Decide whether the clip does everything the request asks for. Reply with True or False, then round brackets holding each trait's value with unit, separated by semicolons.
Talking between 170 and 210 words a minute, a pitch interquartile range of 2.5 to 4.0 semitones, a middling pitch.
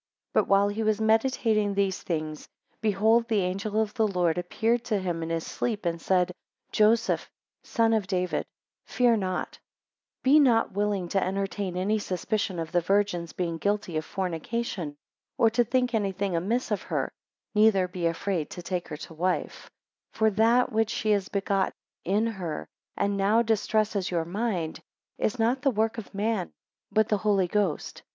False (175 wpm; 3.4 semitones; 200 Hz)